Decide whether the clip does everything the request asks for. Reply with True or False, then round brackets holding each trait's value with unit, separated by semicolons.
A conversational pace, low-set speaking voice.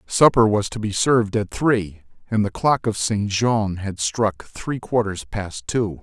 True (190 wpm; 105 Hz)